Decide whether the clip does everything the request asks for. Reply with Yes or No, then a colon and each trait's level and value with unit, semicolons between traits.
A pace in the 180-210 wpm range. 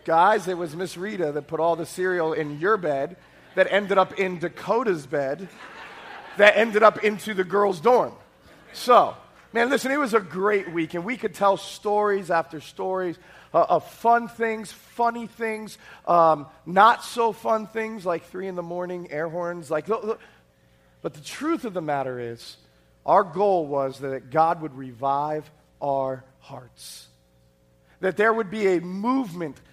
No: average, 170 wpm